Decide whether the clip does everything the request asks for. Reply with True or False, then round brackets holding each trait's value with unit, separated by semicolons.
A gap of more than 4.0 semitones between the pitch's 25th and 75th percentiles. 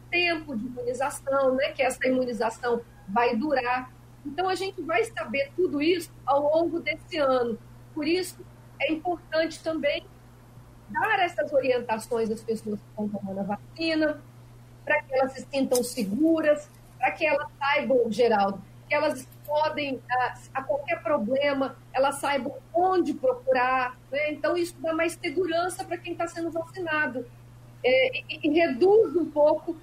True (4.8 semitones)